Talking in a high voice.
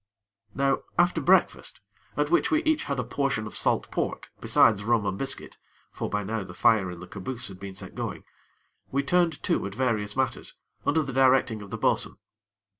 No: low, 120 Hz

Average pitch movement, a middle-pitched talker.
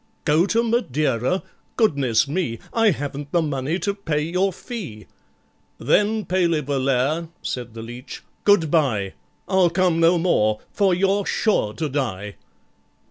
No: wide, 6.3 semitones; medium, 160 Hz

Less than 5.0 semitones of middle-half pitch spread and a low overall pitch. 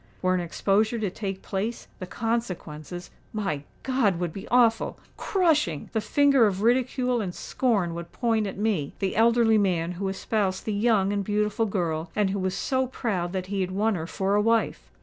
No: average, 3.6 semitones; high, 205 Hz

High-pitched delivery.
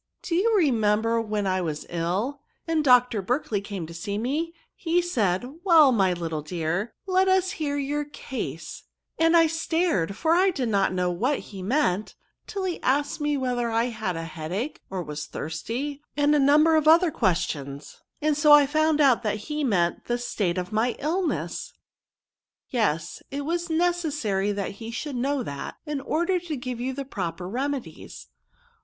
Yes: very high, 250 Hz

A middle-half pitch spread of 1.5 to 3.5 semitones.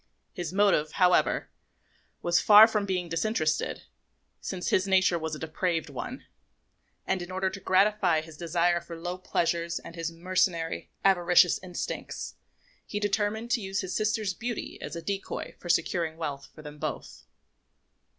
Yes: average, 2.8 semitones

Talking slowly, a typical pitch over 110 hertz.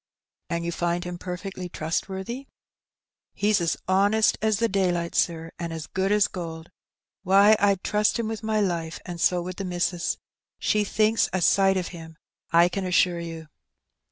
No: average, 170 wpm; medium, 185 Hz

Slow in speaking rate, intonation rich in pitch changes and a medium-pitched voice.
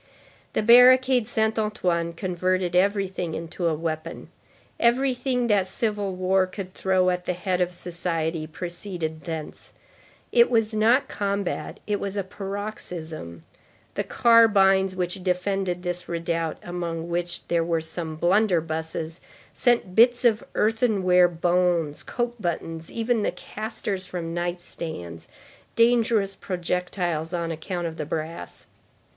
No: slow, 130 wpm; average, 3.8 semitones; medium, 180 Hz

